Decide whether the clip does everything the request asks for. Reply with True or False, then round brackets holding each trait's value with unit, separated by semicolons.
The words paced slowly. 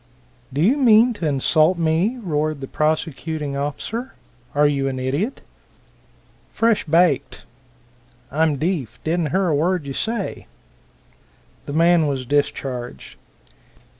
True (125 wpm)